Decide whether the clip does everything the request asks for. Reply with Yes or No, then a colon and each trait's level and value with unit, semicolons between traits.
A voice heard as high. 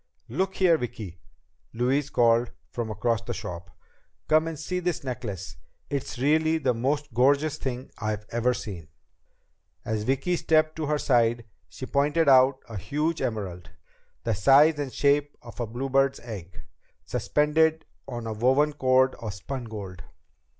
No: low, 130 Hz